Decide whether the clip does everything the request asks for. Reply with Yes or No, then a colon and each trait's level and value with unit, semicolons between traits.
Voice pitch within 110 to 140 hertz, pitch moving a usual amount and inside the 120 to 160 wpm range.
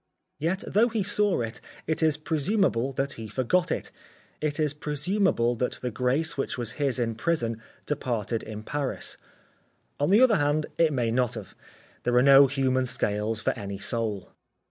No: low, 135 Hz; average, 5.0 semitones; average, 170 wpm